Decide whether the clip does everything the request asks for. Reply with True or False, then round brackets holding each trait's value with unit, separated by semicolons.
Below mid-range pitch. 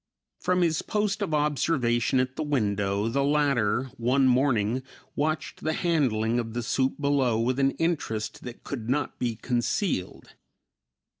True (130 Hz)